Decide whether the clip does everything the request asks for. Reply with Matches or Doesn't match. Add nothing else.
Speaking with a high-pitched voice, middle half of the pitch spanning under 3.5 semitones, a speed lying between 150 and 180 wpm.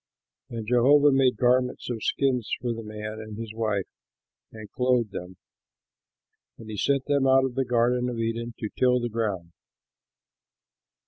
Doesn't match